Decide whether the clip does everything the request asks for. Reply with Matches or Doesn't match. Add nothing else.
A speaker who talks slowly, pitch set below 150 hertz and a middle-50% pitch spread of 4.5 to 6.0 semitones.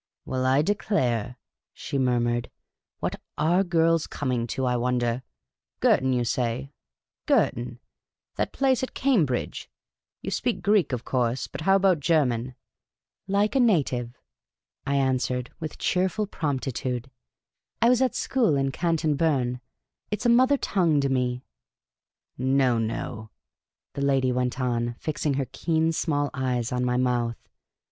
Doesn't match